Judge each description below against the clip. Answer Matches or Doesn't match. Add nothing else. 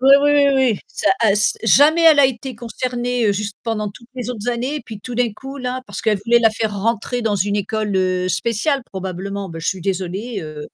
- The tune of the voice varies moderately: Matches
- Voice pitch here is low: Doesn't match